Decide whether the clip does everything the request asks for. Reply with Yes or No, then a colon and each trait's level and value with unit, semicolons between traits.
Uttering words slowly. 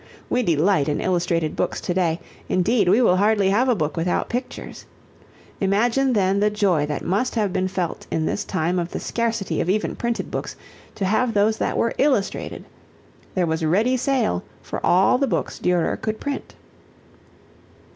No: average, 175 wpm